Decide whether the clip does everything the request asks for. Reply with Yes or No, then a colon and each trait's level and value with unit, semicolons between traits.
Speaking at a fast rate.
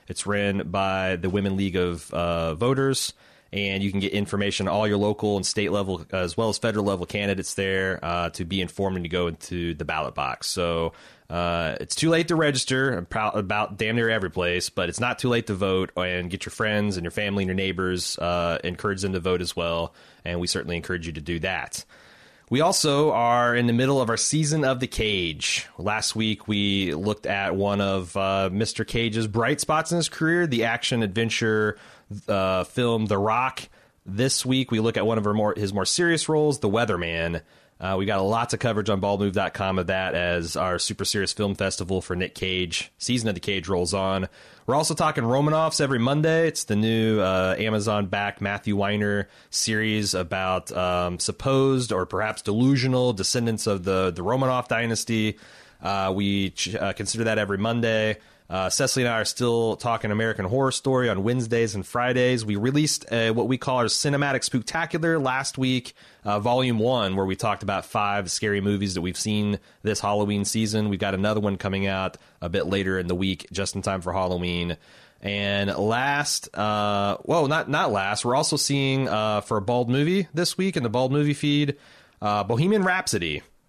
No: average, 195 wpm